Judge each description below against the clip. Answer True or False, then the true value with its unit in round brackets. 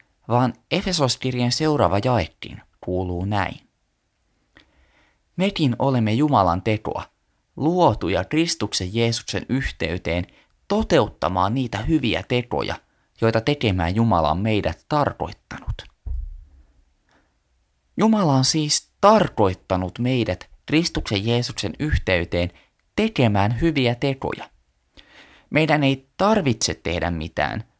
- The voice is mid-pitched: False (110 Hz)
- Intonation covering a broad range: True (7.5 semitones)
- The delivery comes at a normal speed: False (85 wpm)